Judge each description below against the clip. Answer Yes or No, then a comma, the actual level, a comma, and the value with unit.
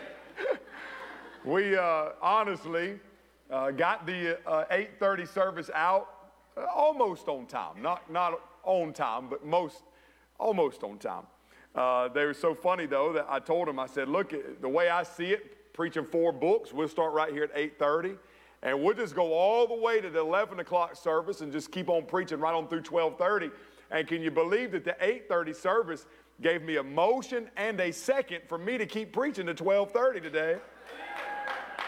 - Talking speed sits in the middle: Yes, average, 175 wpm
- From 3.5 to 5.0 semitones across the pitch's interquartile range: Yes, average, 4.2 semitones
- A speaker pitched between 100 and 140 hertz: No, medium, 175 Hz